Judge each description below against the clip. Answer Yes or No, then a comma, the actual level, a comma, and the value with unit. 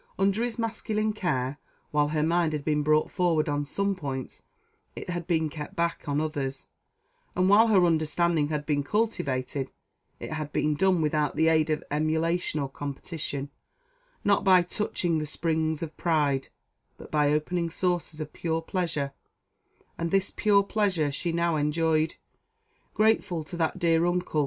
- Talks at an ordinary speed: Yes, average, 160 wpm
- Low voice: No, medium, 160 Hz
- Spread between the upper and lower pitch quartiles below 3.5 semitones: Yes, average, 3.1 semitones